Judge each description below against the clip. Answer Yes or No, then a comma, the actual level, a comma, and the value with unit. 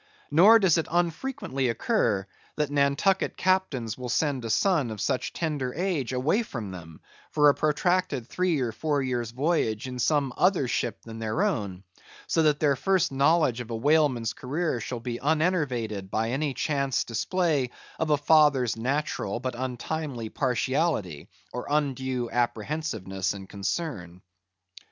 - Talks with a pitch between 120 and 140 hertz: Yes, low, 135 Hz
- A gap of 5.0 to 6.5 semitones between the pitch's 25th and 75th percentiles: Yes, average, 5.3 semitones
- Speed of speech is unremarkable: Yes, average, 150 wpm